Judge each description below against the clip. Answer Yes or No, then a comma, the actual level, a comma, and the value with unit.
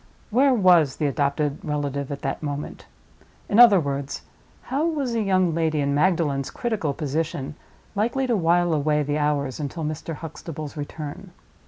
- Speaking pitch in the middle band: Yes, medium, 155 Hz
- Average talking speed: Yes, average, 160 wpm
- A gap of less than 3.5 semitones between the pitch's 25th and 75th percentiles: No, average, 4.5 semitones